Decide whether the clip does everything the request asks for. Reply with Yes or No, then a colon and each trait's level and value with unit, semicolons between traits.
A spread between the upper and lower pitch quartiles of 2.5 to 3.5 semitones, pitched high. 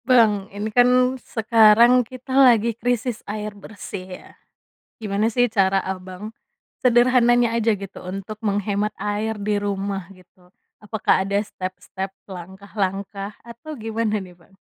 Yes: average, 3.0 semitones; high, 210 Hz